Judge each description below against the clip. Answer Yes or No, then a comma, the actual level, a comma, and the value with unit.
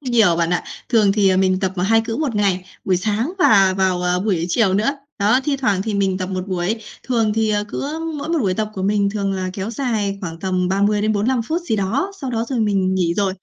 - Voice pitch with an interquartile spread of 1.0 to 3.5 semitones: Yes, average, 3.2 semitones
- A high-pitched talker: Yes, high, 200 Hz